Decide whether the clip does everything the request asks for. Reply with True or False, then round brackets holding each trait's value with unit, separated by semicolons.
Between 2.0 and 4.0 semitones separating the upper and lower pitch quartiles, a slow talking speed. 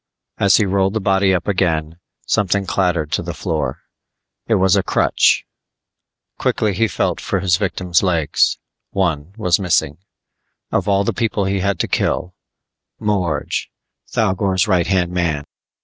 False (2.4 semitones; 150 wpm)